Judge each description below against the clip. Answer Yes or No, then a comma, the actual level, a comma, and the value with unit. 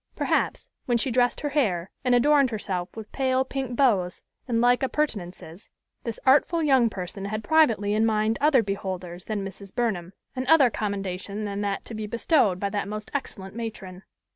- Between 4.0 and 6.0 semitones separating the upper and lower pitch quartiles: Yes, average, 4.6 semitones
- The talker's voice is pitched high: Yes, high, 215 Hz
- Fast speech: No, average, 175 wpm